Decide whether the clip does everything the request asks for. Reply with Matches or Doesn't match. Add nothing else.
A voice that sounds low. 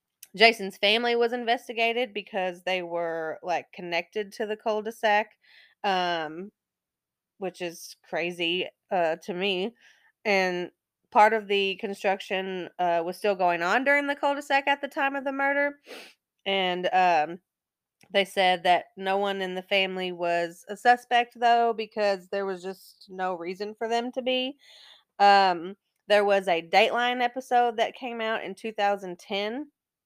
Doesn't match